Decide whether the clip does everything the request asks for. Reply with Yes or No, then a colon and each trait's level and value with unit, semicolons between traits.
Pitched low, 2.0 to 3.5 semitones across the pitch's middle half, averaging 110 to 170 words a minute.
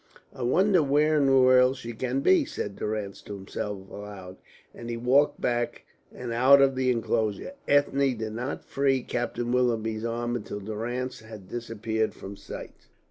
Yes: low, 120 Hz; average, 3.2 semitones; average, 165 wpm